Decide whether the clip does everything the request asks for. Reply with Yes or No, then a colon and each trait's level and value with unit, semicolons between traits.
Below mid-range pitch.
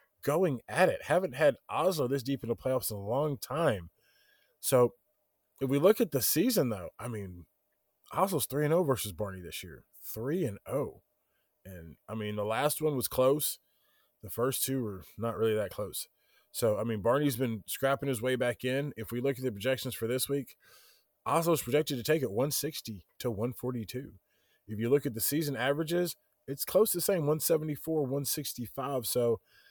Yes: low, 130 Hz